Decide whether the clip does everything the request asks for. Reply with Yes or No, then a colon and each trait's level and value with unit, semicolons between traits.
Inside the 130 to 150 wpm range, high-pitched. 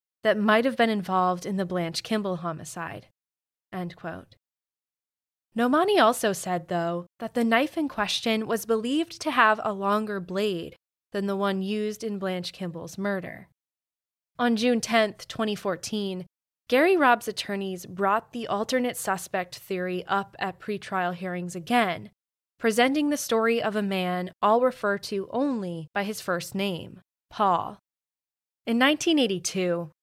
Yes: average, 140 wpm; high, 200 Hz